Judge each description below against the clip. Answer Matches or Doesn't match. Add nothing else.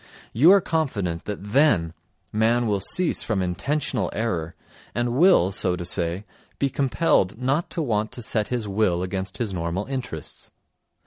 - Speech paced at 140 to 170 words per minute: Matches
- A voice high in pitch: Doesn't match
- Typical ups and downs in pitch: Doesn't match